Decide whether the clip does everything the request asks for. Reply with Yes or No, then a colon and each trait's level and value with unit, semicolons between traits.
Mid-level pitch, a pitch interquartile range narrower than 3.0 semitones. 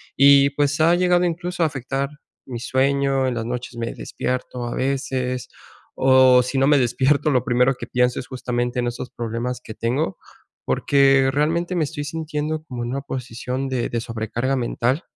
No: low, 130 Hz; narrow, 2.5 semitones